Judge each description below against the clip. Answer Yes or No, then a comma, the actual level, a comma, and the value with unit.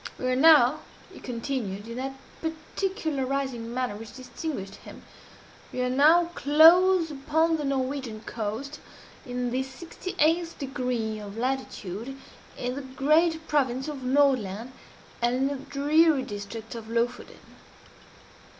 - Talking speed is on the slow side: Yes, slow, 130 wpm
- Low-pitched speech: No, very high, 265 Hz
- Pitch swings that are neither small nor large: Yes, average, 4.1 semitones